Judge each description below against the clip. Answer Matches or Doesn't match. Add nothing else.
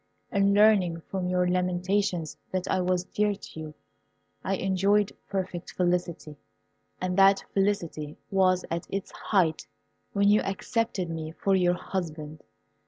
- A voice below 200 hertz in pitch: Matches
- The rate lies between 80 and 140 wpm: Matches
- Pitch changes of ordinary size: Doesn't match